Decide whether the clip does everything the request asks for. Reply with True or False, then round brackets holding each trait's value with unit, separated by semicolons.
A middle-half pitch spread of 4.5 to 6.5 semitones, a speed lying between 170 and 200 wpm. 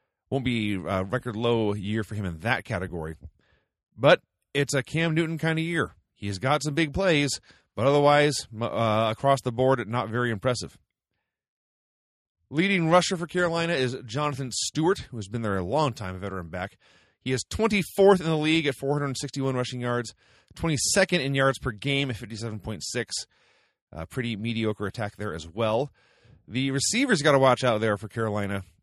True (5.4 semitones; 175 wpm)